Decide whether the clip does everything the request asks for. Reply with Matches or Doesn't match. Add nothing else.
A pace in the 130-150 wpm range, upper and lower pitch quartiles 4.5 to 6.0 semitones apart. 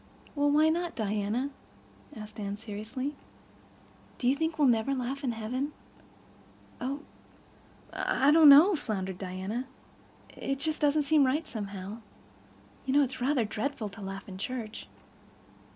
Matches